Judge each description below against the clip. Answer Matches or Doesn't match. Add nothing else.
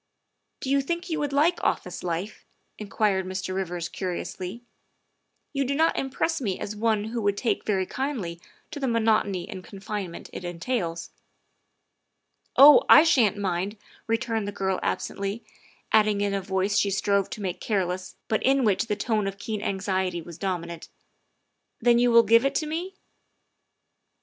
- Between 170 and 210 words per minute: Matches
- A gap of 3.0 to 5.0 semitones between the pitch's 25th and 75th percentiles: Matches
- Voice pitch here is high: Matches